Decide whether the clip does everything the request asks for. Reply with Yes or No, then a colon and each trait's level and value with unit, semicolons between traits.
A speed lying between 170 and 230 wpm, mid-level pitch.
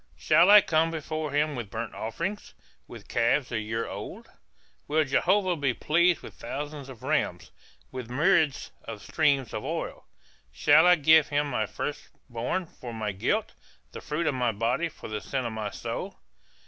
Yes: average, 175 wpm; medium, 145 Hz